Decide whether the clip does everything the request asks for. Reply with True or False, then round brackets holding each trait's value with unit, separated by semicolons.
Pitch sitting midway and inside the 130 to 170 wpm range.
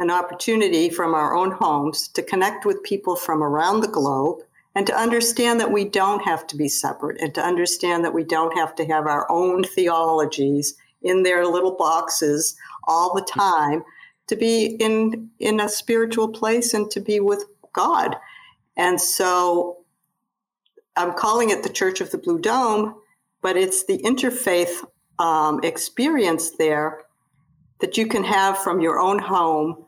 True (180 Hz; 165 wpm)